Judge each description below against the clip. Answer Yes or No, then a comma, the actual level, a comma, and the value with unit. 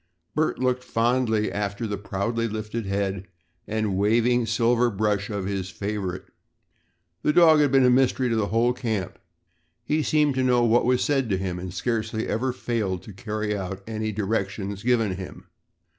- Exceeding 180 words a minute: No, average, 170 wpm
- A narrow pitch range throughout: No, average, 3.6 semitones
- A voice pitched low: Yes, low, 110 Hz